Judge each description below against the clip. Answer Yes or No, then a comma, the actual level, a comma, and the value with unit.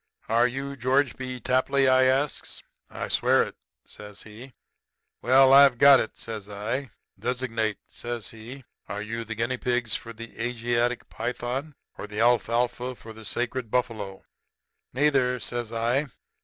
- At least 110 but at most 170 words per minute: Yes, average, 145 wpm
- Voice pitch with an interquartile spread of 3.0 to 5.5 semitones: No, narrow, 2.4 semitones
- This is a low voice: Yes, low, 120 Hz